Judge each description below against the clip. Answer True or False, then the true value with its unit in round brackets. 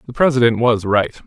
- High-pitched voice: False (120 Hz)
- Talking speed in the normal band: True (190 wpm)